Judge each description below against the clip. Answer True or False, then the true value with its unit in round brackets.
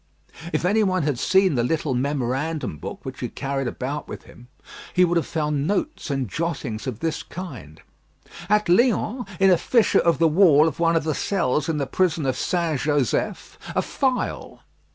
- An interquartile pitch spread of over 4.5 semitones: True (4.9 semitones)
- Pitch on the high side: False (160 Hz)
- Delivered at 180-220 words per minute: True (185 wpm)